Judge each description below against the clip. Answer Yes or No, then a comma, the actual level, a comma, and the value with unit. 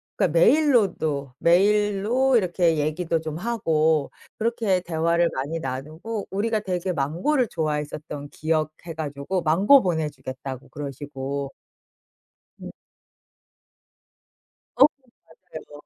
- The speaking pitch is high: No, medium, 165 Hz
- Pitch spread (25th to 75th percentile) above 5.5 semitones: No, average, 5.2 semitones